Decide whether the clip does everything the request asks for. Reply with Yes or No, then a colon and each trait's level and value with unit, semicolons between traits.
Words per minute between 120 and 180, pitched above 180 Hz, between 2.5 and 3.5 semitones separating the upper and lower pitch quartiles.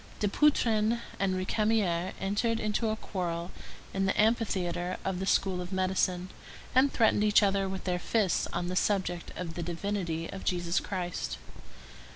Yes: average, 155 wpm; high, 190 Hz; average, 3.0 semitones